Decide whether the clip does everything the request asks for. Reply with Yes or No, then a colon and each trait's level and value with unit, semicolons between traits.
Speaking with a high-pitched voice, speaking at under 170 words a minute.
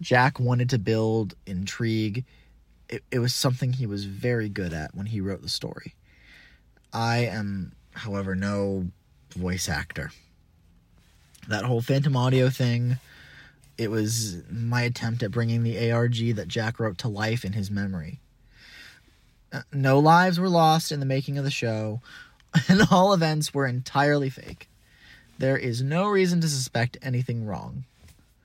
No: low, 115 Hz; average, 150 wpm